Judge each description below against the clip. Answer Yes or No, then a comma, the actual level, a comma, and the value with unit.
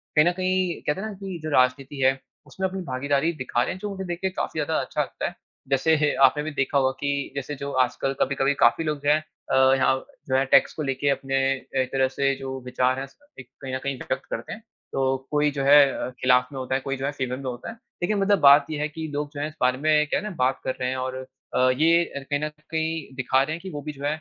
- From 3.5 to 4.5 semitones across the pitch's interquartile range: No, average, 2.9 semitones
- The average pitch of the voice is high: No, medium, 140 Hz